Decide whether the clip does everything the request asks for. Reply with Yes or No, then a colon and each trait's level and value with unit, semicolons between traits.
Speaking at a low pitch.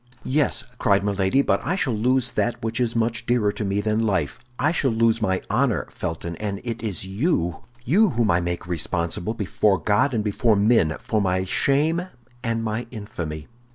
Yes: low, 110 Hz